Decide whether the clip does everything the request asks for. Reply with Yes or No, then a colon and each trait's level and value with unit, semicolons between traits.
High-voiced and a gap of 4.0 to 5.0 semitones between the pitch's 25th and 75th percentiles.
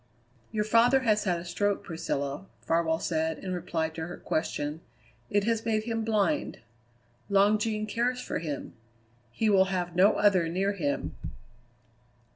Yes: high, 195 Hz; average, 4.7 semitones